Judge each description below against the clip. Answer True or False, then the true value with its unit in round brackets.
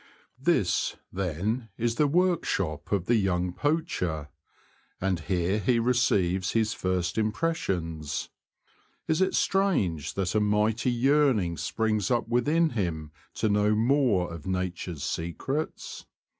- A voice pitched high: False (105 Hz)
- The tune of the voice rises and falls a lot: True (6.0 semitones)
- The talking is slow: True (125 wpm)